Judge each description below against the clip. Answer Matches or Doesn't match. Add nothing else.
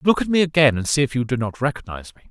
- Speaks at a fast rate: Matches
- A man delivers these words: Matches